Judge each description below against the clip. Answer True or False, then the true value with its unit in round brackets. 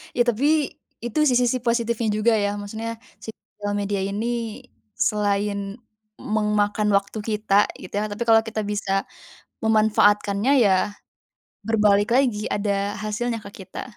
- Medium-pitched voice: False (210 Hz)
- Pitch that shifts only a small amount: True (2.2 semitones)